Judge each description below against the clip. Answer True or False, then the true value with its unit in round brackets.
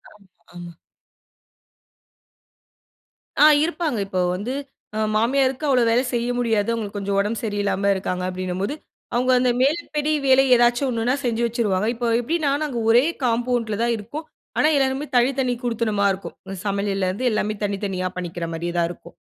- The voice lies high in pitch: True (230 Hz)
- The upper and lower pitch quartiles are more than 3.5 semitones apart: True (4.2 semitones)